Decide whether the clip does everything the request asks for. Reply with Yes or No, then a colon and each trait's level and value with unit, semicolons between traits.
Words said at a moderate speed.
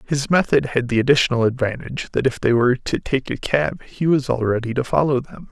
No: fast, 230 wpm